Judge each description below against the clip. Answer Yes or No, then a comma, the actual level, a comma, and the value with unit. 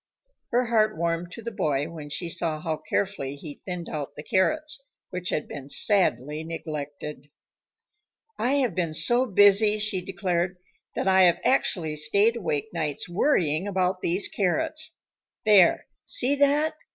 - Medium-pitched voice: Yes, medium, 180 Hz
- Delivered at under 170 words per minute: Yes, average, 150 wpm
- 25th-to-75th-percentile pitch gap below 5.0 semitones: No, wide, 5.5 semitones